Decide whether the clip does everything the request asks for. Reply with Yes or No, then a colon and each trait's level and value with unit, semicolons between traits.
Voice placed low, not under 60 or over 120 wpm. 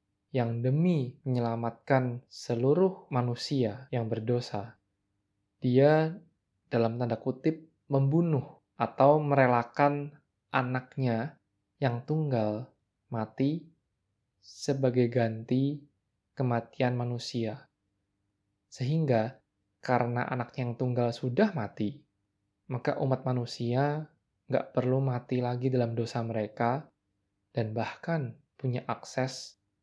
Yes: low, 125 Hz; slow, 85 wpm